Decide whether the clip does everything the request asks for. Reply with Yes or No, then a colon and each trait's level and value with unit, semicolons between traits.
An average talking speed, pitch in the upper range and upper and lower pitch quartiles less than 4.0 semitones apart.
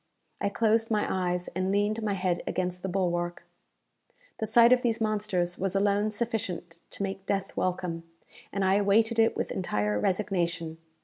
Yes: average, 165 wpm; high, 195 Hz; average, 3.1 semitones